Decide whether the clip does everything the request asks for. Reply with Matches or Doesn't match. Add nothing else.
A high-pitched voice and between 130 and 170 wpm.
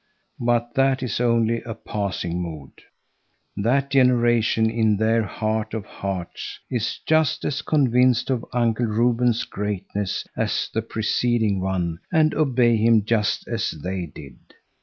Doesn't match